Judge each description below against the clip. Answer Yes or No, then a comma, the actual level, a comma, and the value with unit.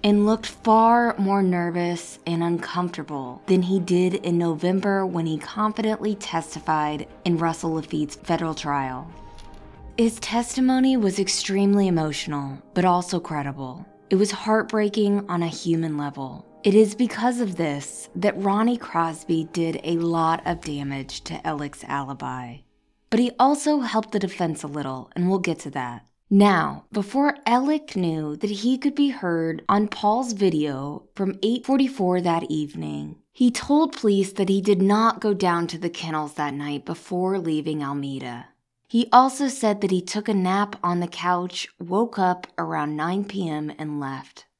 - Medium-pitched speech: Yes, medium, 180 Hz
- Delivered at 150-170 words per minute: Yes, average, 155 wpm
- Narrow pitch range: No, average, 5.3 semitones